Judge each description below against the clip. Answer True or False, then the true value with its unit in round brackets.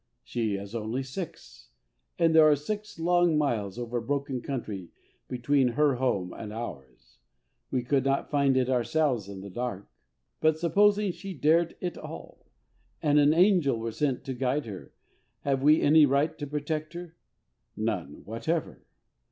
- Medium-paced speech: True (155 wpm)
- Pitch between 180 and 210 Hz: False (140 Hz)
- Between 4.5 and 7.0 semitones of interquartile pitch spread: True (5.0 semitones)